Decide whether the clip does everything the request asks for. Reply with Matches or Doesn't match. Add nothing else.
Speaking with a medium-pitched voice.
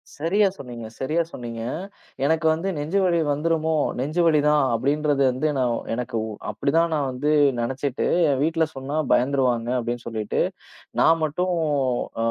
Matches